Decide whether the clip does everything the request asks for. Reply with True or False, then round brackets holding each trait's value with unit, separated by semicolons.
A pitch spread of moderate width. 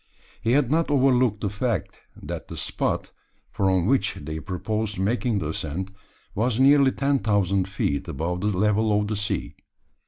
True (4.7 semitones)